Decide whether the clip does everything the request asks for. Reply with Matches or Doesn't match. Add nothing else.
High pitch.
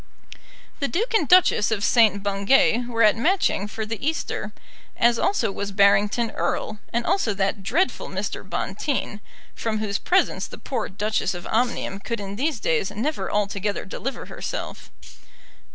Matches